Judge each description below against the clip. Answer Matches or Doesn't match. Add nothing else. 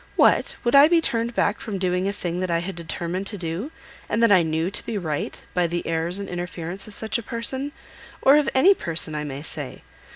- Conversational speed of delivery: Doesn't match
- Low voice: Doesn't match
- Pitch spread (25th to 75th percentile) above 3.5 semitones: Matches